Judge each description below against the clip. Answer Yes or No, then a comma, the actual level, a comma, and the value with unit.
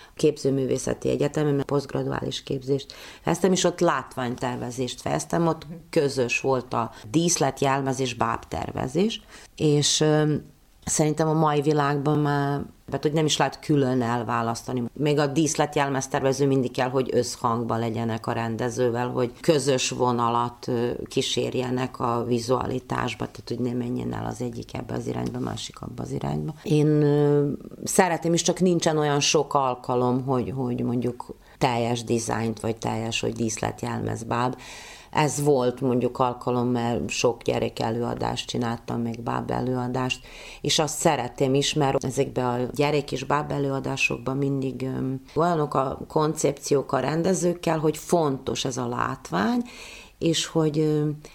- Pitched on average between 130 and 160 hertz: Yes, low, 135 Hz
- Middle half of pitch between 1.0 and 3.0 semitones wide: No, average, 3.6 semitones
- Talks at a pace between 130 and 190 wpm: Yes, average, 135 wpm